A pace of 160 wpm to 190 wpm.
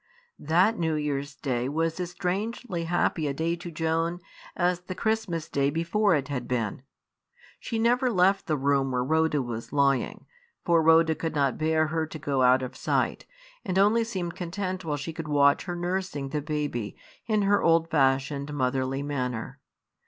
Yes: average, 175 wpm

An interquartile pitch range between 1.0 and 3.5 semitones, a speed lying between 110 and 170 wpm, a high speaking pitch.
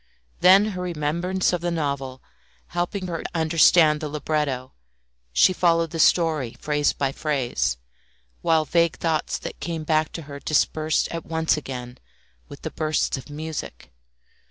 No: narrow, 2.4 semitones; average, 150 wpm; medium, 155 Hz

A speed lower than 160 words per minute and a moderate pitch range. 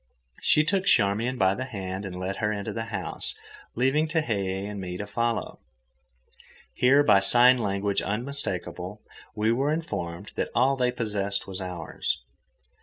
Yes: average, 150 wpm; average, 4.7 semitones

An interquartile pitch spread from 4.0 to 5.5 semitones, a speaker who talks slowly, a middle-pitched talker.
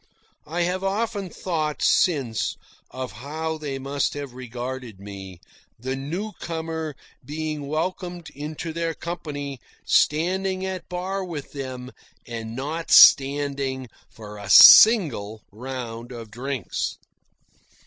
Yes: average, 4.9 semitones; slow, 110 wpm; medium, 145 Hz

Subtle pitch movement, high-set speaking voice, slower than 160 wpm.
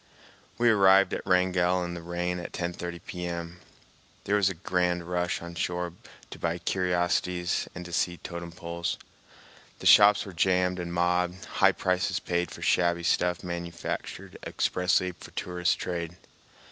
No: narrow, 0.9 semitones; very low, 90 Hz; average, 145 wpm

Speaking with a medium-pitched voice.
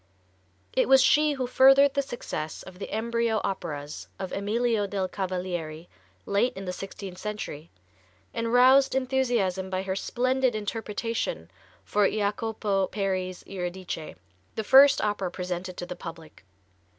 No: high, 205 Hz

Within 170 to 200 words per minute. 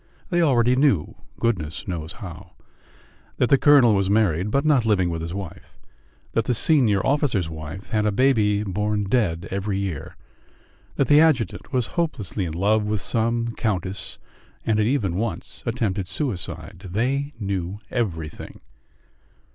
No: average, 145 wpm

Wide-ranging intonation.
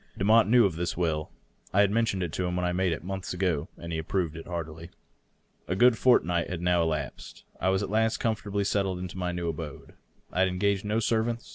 No: average, 3.2 semitones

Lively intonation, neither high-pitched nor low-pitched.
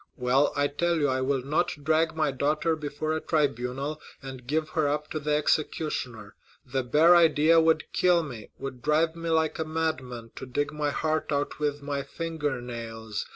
No: average, 3.1 semitones; medium, 150 Hz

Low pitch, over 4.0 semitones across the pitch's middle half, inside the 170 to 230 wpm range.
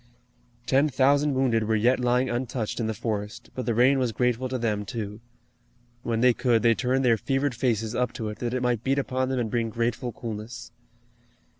No: low, 120 Hz; narrow, 2.4 semitones; average, 200 wpm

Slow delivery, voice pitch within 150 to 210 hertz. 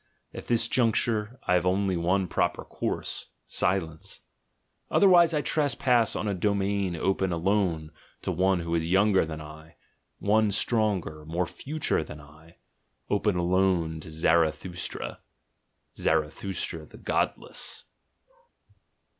No: slow, 120 wpm; very low, 95 Hz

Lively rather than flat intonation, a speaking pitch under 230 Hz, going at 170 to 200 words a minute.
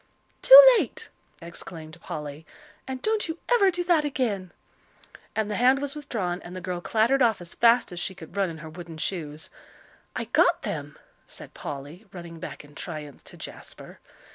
Yes: wide, 8.4 semitones; high, 190 Hz; average, 175 wpm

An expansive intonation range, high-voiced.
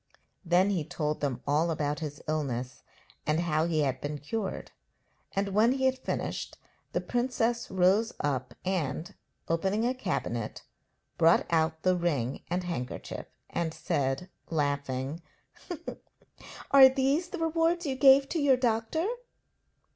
No: wide, 8.5 semitones; medium, 175 Hz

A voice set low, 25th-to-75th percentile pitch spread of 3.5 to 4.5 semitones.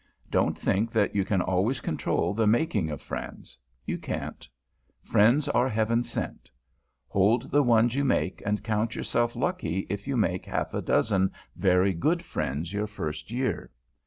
Yes: low, 105 Hz; average, 4.1 semitones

